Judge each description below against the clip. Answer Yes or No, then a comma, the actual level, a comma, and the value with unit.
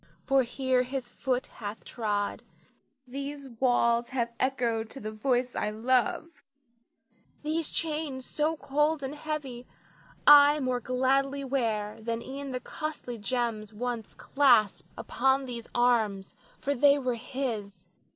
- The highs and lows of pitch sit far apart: No, average, 3.1 semitones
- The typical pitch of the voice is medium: No, very high, 255 Hz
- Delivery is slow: Yes, slow, 130 wpm